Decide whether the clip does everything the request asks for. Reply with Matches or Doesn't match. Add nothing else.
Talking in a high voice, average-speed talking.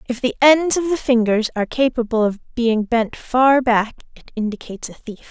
Matches